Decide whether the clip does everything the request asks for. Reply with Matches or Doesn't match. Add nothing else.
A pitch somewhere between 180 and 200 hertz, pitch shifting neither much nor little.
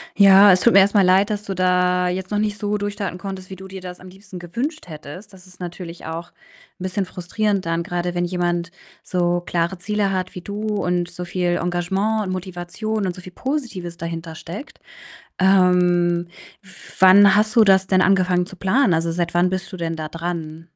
Doesn't match